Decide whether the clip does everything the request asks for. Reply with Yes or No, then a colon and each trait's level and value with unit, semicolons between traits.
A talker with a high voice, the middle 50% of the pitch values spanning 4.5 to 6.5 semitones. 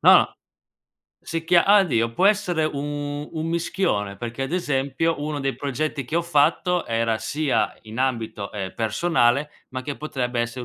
No: medium, 145 Hz; wide, 5.5 semitones